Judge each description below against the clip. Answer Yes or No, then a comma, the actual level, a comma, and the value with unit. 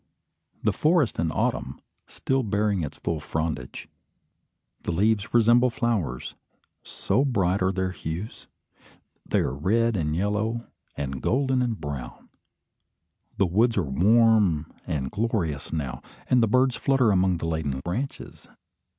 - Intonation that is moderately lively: No, wide, 6.6 semitones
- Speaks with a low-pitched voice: Yes, low, 100 Hz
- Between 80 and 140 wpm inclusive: Yes, slow, 135 wpm